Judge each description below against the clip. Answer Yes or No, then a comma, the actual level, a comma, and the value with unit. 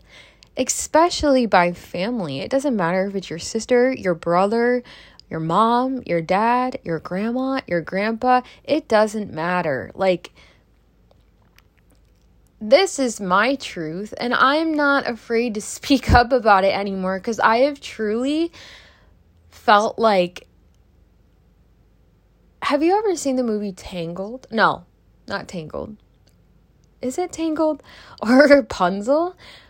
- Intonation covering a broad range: Yes, wide, 6.4 semitones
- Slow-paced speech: Yes, slow, 120 wpm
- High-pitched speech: Yes, high, 225 Hz